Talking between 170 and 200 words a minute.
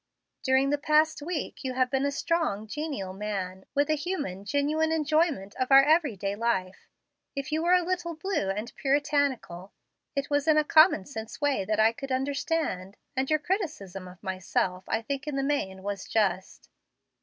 Yes: average, 180 wpm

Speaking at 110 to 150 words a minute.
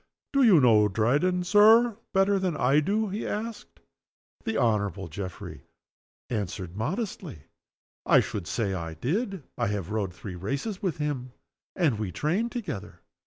Yes: average, 145 wpm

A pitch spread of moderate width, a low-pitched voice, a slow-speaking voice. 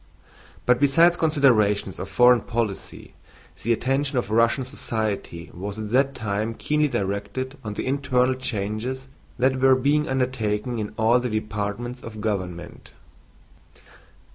Yes: average, 3.9 semitones; low, 120 Hz; slow, 130 wpm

